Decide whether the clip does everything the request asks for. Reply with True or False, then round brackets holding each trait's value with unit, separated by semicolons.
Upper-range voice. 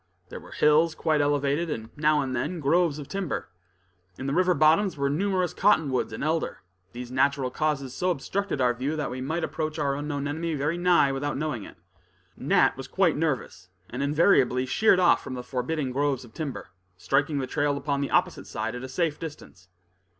False (145 Hz)